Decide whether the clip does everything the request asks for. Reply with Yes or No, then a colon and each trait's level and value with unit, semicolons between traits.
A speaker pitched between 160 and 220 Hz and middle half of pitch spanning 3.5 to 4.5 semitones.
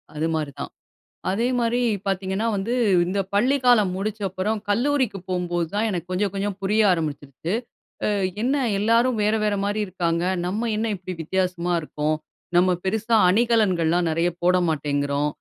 Yes: high, 190 Hz; average, 4.1 semitones